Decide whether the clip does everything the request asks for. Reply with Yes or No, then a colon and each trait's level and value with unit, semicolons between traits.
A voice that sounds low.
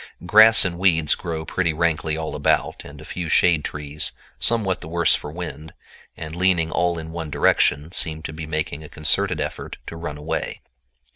Yes: very low, 80 Hz